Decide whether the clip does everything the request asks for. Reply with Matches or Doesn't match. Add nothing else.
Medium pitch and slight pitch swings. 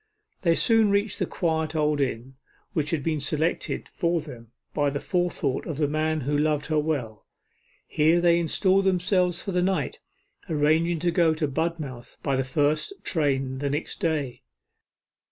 Doesn't match